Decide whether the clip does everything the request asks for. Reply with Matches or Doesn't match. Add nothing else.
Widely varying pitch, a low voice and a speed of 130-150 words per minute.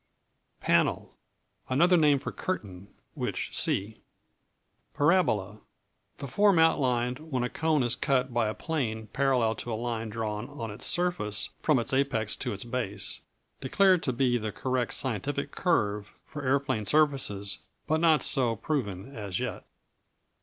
Doesn't match